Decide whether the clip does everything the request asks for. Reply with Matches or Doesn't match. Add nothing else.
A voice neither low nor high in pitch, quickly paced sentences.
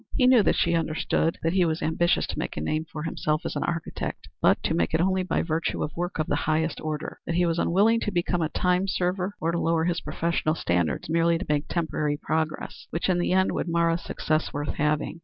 Matches